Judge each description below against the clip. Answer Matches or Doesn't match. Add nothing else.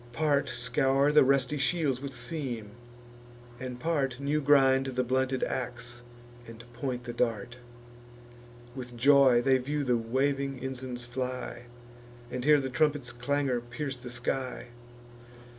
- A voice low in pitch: Matches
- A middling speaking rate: Doesn't match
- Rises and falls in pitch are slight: Matches